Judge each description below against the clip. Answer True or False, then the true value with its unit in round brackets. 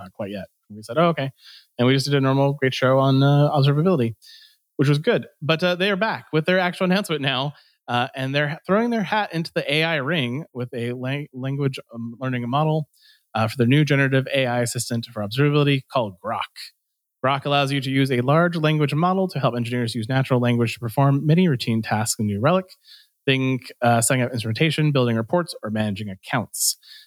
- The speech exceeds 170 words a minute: True (200 wpm)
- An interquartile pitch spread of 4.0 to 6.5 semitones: True (4.8 semitones)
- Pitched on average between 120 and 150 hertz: True (140 Hz)